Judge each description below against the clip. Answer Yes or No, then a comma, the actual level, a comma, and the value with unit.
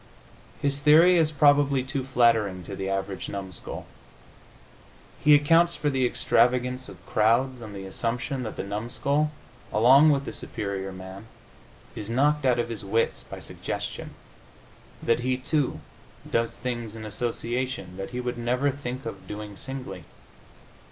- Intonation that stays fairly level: No, average, 4.5 semitones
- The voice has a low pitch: Yes, low, 125 Hz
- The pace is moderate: Yes, average, 145 wpm